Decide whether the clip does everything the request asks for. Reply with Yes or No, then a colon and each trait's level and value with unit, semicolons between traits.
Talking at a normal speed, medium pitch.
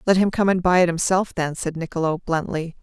No: fast, 235 wpm; medium, 175 Hz